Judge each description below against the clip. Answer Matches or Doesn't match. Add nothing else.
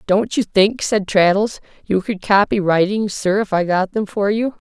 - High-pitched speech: Matches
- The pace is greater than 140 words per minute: Matches